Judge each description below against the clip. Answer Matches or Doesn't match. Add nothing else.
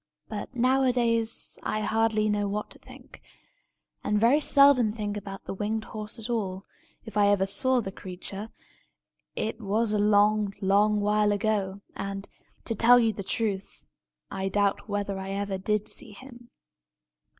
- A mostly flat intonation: Matches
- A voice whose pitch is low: Doesn't match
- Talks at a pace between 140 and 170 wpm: Matches